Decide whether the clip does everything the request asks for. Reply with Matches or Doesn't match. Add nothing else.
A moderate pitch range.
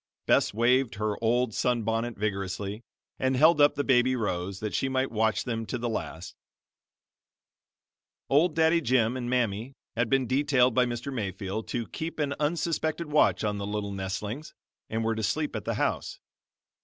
Matches